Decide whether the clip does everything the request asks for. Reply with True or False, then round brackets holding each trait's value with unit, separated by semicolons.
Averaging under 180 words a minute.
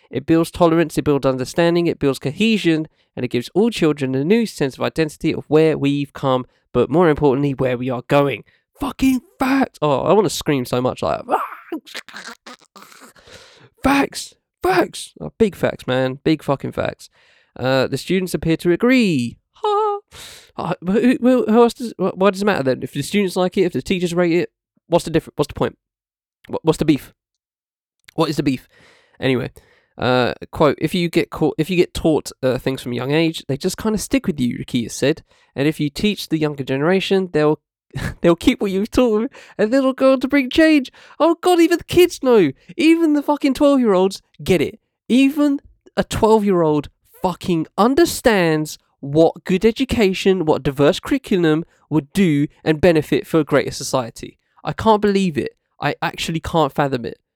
False (185 wpm)